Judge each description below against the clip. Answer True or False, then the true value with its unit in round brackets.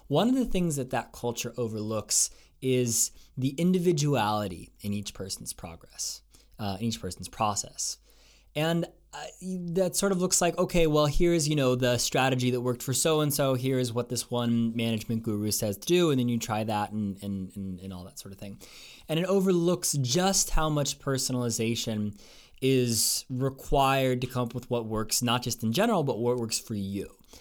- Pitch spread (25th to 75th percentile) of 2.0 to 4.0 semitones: False (5.4 semitones)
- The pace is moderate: True (190 wpm)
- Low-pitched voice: True (125 Hz)